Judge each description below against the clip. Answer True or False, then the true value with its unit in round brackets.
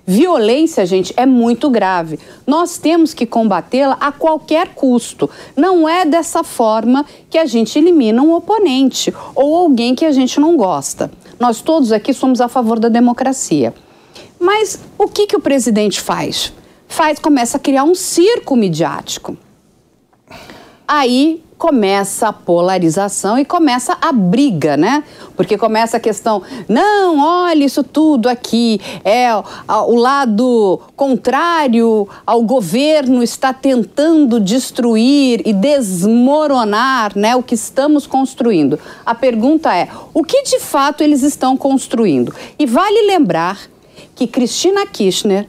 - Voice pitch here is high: True (265 Hz)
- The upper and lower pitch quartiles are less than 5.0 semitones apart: False (5.3 semitones)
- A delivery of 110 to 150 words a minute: True (135 wpm)